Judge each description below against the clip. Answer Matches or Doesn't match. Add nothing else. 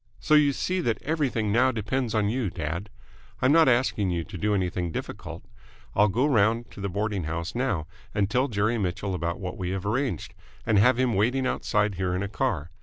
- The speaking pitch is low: Matches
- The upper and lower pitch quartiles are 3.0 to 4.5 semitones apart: Doesn't match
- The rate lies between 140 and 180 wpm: Doesn't match